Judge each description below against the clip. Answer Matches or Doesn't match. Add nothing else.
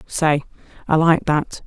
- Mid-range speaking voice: Matches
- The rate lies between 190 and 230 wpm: Doesn't match